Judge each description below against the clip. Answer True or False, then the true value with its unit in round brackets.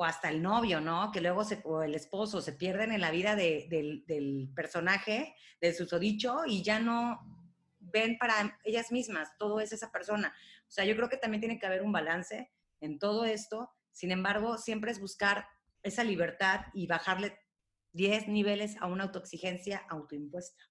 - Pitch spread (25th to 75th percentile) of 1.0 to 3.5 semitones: False (4.1 semitones)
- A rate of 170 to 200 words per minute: True (180 wpm)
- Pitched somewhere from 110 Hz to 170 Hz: False (200 Hz)